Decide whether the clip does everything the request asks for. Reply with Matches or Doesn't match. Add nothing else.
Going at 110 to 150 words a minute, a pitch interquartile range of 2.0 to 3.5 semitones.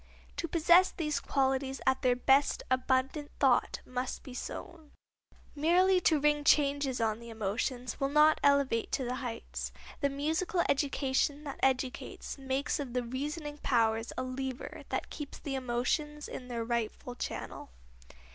Matches